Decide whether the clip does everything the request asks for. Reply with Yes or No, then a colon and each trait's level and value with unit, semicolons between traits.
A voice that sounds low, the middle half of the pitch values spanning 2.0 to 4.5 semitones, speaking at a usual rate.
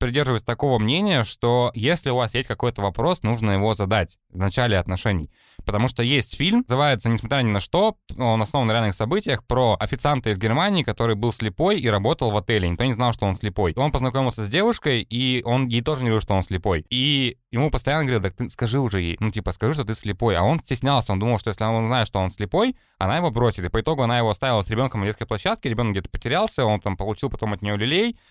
No: low, 120 Hz; average, 4.0 semitones; fast, 235 wpm